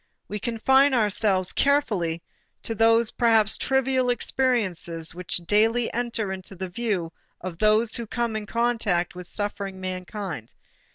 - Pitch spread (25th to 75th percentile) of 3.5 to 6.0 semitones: Yes, average, 4.2 semitones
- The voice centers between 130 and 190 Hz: No, high, 215 Hz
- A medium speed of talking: No, slow, 130 wpm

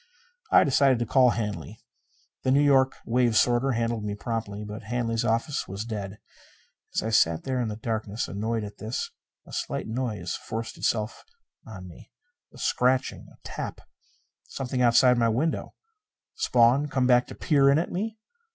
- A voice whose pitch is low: Yes, low, 115 Hz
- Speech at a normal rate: Yes, average, 165 wpm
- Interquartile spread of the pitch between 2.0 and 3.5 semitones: Yes, average, 3.0 semitones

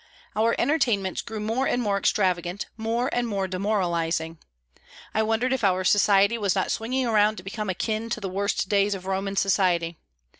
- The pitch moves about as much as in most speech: Yes, average, 3.0 semitones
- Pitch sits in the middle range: No, high, 200 Hz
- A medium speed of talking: Yes, average, 175 wpm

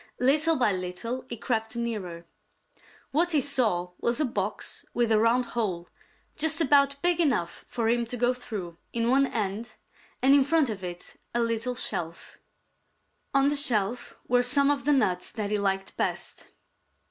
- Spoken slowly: No, average, 170 wpm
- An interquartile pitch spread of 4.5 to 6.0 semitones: Yes, average, 4.9 semitones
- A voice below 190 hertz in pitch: No, high, 235 Hz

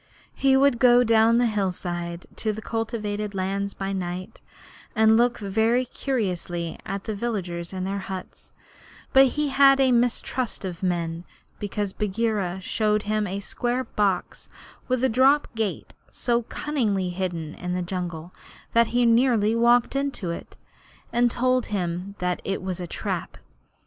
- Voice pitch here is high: Yes, high, 210 Hz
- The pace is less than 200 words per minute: Yes, average, 150 wpm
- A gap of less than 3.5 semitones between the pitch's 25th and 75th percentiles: No, average, 4.5 semitones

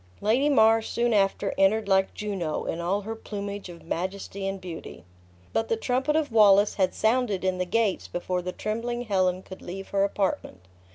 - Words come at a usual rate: Yes, average, 180 wpm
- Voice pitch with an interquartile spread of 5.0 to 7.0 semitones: No, average, 3.1 semitones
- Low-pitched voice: No, high, 200 Hz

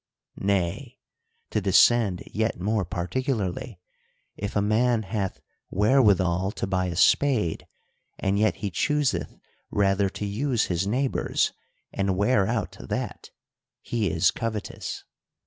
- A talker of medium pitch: No, low, 100 Hz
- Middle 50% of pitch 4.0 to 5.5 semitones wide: No, average, 3.4 semitones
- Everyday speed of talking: No, slow, 125 wpm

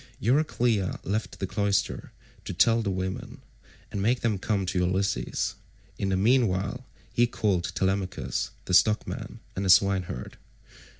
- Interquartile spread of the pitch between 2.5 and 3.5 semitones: Yes, average, 2.9 semitones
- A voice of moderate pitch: No, low, 100 Hz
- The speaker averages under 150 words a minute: Yes, slow, 135 wpm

